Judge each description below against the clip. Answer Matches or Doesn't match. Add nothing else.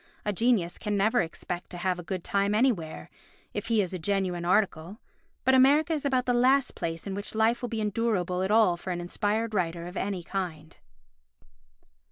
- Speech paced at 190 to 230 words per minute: Matches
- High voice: Matches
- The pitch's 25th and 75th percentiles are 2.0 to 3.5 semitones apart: Doesn't match